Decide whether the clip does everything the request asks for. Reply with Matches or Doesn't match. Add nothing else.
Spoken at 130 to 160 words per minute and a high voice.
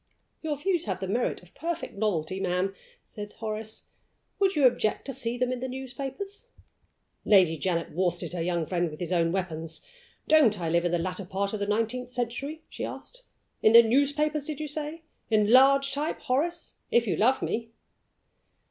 Doesn't match